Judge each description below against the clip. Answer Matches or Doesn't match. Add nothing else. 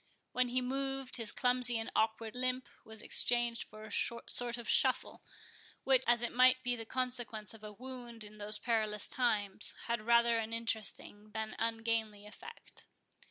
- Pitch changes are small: Matches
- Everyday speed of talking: Matches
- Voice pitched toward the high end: Matches